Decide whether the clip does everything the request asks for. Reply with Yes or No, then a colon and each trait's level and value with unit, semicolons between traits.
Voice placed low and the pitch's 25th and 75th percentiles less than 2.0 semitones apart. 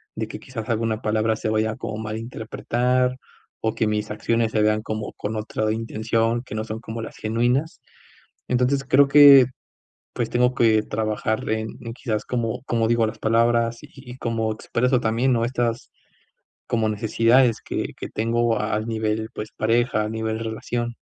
Yes: low, 115 Hz; narrow, 1.6 semitones